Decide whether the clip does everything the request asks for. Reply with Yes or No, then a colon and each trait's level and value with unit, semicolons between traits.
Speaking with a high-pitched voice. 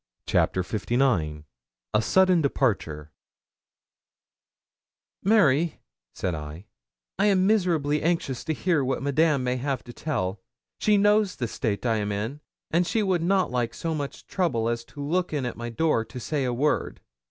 No: medium, 140 Hz